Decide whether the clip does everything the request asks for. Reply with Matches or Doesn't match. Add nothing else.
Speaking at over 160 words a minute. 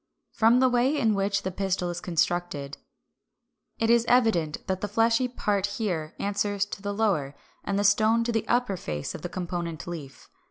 Matches